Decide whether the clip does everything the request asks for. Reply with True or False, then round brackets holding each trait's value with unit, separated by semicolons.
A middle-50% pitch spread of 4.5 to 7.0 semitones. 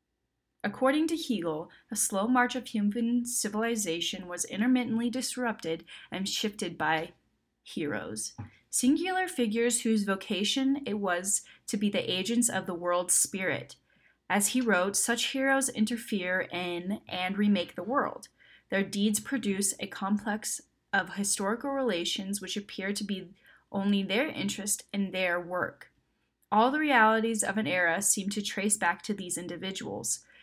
False (3.9 semitones)